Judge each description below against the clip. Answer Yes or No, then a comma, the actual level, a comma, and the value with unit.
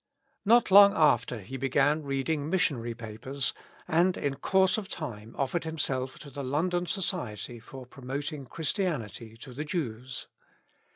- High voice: No, medium, 140 Hz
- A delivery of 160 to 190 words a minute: No, slow, 135 wpm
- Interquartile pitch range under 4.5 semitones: No, average, 5.0 semitones